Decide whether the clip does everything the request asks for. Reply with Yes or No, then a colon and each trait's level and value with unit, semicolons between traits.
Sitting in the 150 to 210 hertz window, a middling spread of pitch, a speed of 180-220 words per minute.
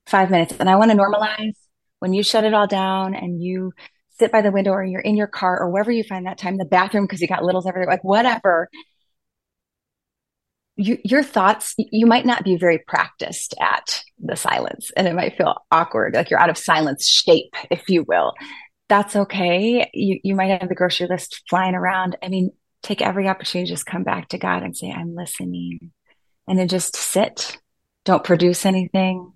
No: high, 190 Hz; narrow, 2.2 semitones; average, 200 wpm